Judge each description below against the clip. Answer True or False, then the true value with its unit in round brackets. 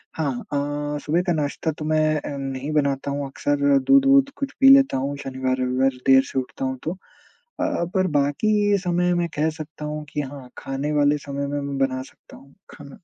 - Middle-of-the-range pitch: True (145 Hz)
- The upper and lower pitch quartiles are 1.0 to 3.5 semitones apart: True (2.5 semitones)